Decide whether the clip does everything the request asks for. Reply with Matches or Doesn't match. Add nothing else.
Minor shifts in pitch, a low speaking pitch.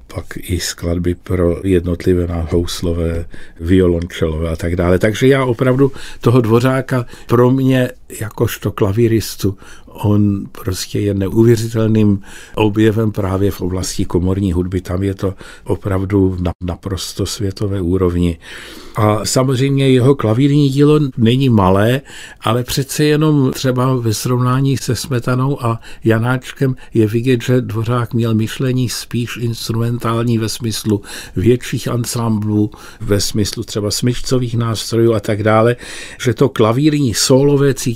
Doesn't match